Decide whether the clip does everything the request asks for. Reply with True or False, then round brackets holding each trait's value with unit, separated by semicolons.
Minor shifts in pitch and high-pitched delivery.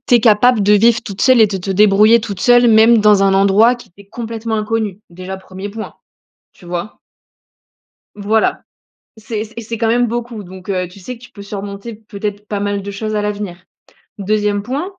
True (2.3 semitones; 210 Hz)